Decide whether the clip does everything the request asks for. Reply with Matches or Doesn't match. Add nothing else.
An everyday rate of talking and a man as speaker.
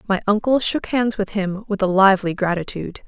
Doesn't match